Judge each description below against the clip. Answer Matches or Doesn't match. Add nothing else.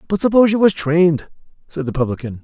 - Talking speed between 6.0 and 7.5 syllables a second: Matches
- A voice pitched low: Doesn't match